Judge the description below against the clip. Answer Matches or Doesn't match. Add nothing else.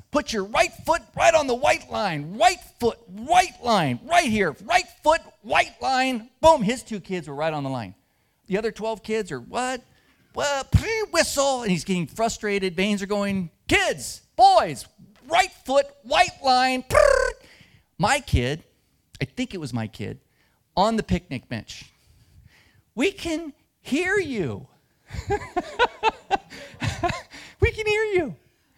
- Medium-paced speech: Matches